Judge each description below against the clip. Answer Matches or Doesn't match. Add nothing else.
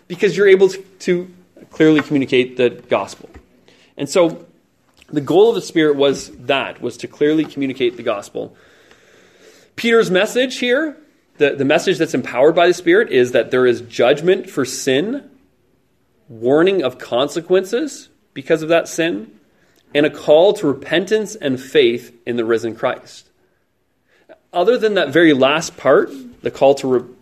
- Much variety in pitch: Matches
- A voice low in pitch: Doesn't match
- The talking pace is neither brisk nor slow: Matches